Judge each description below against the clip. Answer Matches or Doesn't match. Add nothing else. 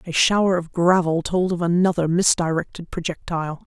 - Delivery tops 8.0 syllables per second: Doesn't match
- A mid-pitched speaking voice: Matches